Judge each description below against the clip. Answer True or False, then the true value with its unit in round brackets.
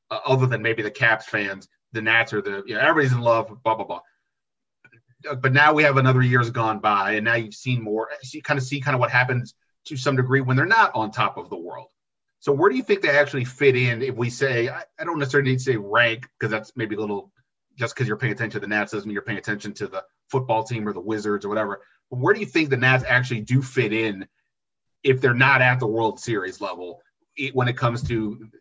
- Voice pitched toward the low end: True (125 Hz)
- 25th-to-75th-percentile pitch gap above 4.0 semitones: False (3.3 semitones)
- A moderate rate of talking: False (255 wpm)